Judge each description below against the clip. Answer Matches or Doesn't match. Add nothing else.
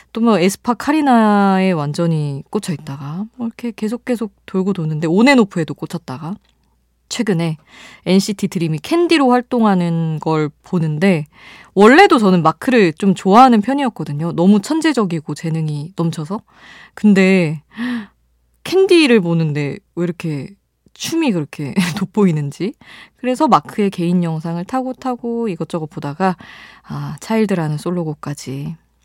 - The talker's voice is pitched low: Doesn't match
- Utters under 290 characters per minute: Doesn't match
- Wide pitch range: Matches